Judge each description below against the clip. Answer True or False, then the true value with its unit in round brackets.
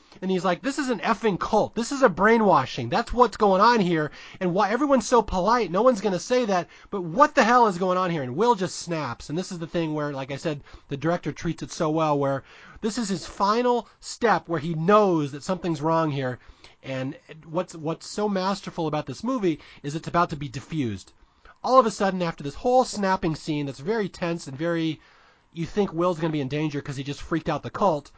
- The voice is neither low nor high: True (175 Hz)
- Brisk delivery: True (235 wpm)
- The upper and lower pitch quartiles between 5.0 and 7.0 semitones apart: True (5.6 semitones)